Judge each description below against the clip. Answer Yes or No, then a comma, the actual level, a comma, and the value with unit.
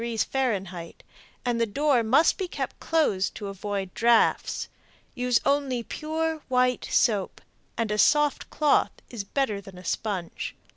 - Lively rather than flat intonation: Yes, wide, 5.7 semitones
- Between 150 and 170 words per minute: No, average, 140 wpm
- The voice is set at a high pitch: Yes, high, 235 Hz